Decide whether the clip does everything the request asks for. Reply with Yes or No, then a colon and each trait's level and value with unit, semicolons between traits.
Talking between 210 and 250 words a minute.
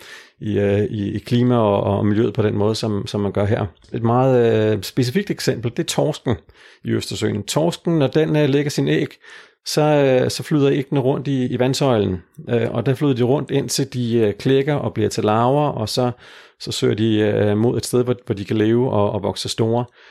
Yes: average, 220 wpm